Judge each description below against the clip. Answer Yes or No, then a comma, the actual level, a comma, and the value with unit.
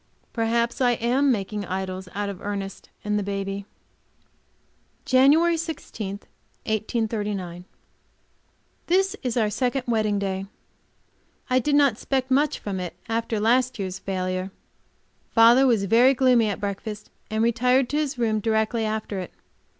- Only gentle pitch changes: No, average, 4.1 semitones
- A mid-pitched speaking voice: No, high, 220 Hz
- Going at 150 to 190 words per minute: No, slow, 135 wpm